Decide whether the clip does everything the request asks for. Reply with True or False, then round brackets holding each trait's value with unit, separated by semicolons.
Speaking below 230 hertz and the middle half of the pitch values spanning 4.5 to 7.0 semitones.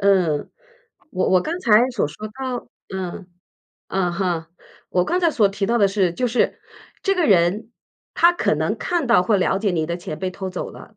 True (195 Hz; 4.8 semitones)